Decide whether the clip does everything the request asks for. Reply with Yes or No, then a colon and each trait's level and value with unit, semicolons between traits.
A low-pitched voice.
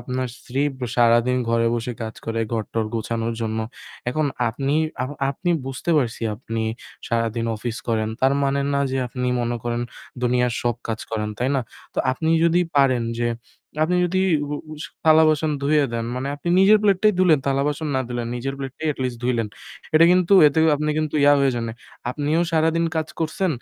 Yes: low, 130 Hz